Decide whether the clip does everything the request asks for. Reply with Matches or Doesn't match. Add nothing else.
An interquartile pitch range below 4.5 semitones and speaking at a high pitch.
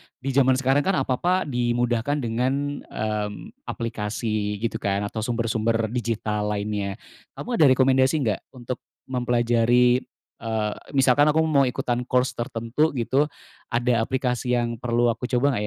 Doesn't match